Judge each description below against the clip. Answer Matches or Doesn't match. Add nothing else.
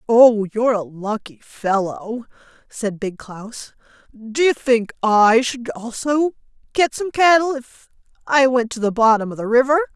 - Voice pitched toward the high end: Matches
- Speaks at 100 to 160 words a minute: Matches